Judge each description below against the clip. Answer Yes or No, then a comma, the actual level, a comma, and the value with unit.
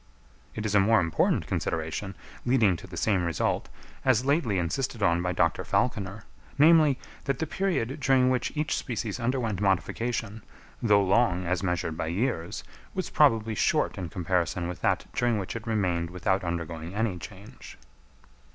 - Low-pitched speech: Yes, low, 105 Hz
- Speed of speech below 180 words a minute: Yes, average, 160 wpm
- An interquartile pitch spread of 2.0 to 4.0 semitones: No, wide, 5.5 semitones